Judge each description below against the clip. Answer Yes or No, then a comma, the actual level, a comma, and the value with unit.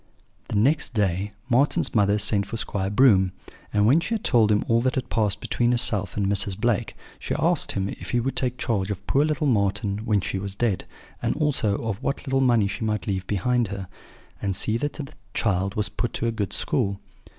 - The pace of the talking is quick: Yes, fast, 215 wpm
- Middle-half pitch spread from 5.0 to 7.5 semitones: No, average, 3.5 semitones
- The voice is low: Yes, low, 105 Hz